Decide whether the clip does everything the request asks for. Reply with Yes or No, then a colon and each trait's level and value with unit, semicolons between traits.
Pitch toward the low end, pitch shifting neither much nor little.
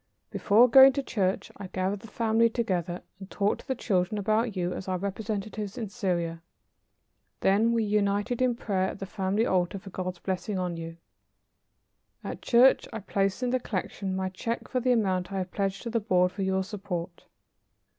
No: high, 200 Hz; average, 3.2 semitones